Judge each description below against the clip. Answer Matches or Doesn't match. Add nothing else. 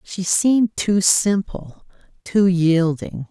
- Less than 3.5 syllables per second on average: Matches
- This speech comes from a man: Doesn't match